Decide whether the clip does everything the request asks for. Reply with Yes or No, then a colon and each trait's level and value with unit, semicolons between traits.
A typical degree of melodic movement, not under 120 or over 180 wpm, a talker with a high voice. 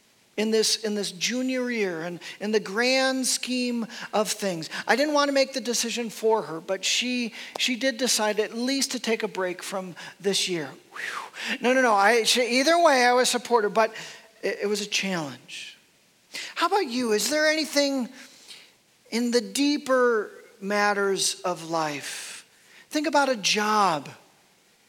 Yes: average, 4.4 semitones; average, 170 wpm; high, 225 Hz